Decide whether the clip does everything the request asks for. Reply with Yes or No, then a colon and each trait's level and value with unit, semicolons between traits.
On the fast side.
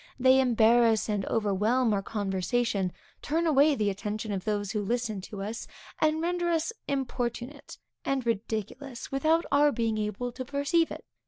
No: average, 155 wpm